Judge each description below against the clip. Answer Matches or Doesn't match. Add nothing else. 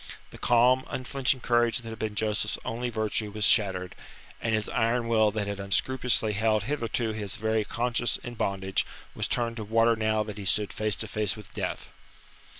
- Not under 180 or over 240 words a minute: Matches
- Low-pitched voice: Matches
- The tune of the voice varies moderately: Doesn't match